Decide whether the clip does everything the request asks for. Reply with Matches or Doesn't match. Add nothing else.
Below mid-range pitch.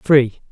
Matches